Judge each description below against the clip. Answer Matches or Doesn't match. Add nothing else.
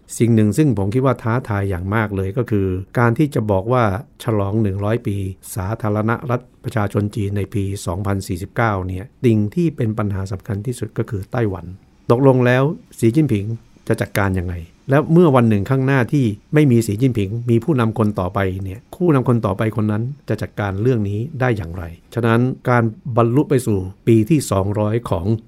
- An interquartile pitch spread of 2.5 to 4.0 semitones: Matches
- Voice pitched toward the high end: Doesn't match